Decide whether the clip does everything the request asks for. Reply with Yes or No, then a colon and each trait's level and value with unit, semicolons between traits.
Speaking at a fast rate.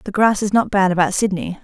Yes: fast, 260 wpm